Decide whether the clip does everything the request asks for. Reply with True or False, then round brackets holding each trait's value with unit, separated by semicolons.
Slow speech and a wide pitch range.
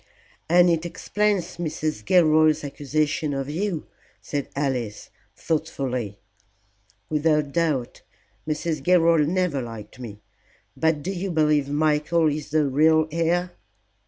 False (115 wpm; 2.8 semitones)